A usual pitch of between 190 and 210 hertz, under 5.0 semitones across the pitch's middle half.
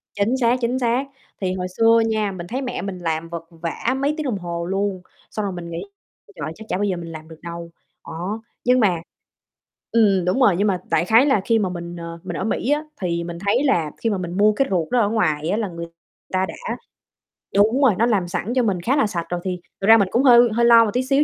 No: high, 200 Hz; average, 5.3 semitones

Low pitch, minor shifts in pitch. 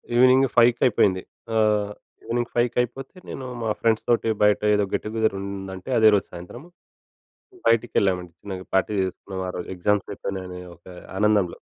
No: low, 105 Hz; average, 3.6 semitones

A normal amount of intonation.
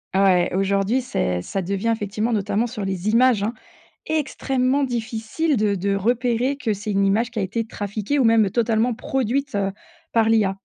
Yes: average, 3.5 semitones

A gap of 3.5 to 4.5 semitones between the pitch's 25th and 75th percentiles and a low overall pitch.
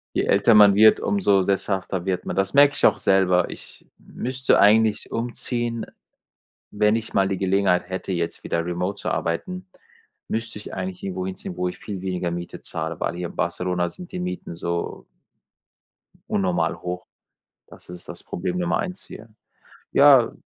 Yes: average, 3.8 semitones; very low, 95 Hz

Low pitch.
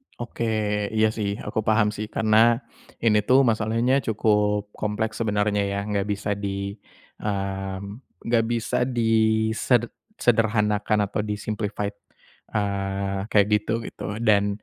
Yes: low, 105 Hz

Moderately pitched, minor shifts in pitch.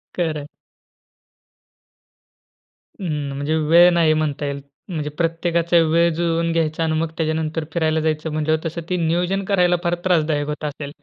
Yes: medium, 160 Hz; narrow, 1.7 semitones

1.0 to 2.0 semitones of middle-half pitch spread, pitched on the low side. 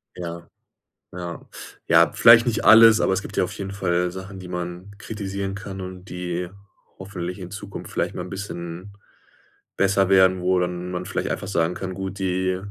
Yes: narrow, 1.6 semitones; very low, 95 Hz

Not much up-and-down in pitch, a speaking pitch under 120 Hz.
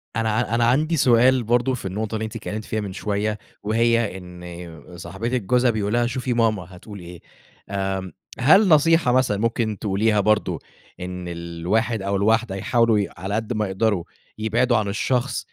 No: average, 3.2 semitones; low, 110 Hz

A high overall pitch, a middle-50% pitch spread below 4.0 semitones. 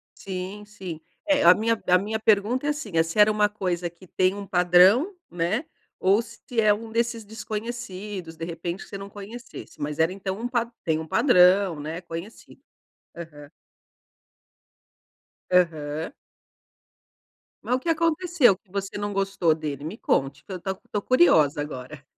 No: high, 195 Hz; average, 4.6 semitones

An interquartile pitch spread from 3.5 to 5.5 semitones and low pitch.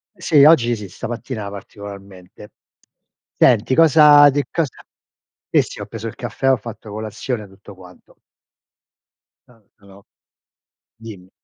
Yes: average, 5.0 semitones; low, 110 Hz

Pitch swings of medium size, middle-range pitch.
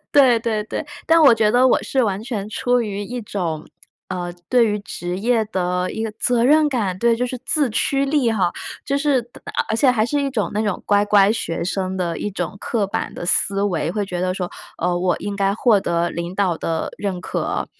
No: average, 4.8 semitones; high, 205 Hz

